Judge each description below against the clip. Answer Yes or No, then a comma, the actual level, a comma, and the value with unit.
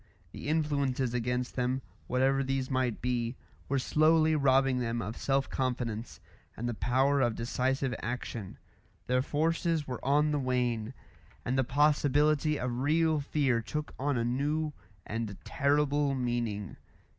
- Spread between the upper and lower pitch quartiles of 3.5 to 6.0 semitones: No, average, 3.0 semitones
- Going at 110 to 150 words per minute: Yes, average, 140 wpm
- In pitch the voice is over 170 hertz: No, low, 130 Hz